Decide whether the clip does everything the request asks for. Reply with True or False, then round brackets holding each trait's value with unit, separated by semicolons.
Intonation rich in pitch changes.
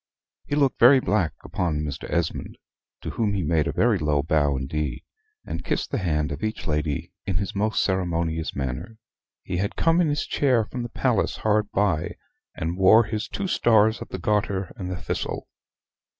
True (5.9 semitones)